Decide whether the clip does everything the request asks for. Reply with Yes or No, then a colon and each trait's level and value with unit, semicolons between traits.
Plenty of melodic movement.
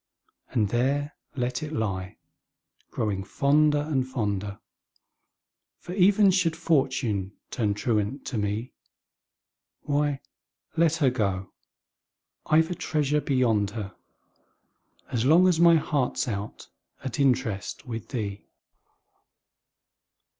Yes: wide, 6.2 semitones